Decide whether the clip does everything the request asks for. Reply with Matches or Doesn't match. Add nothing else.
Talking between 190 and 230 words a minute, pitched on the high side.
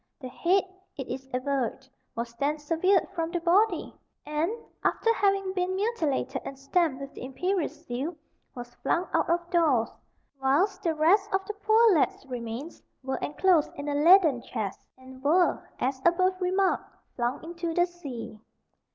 Doesn't match